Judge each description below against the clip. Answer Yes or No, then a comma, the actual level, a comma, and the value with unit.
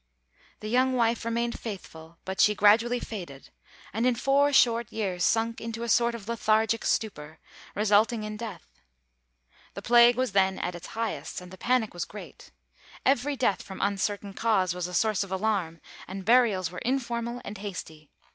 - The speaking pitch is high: Yes, high, 215 Hz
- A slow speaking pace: No, average, 170 wpm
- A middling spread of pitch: Yes, average, 3.7 semitones